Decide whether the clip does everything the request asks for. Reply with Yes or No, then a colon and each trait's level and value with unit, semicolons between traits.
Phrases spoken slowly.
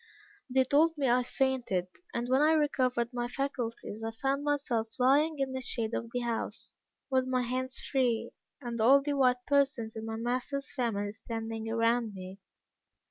No: average, 170 wpm